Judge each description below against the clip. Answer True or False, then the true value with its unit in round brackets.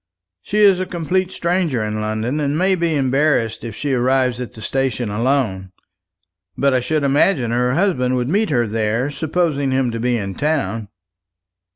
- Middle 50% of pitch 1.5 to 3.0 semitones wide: False (5.1 semitones)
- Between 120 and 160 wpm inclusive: False (175 wpm)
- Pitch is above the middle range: False (130 Hz)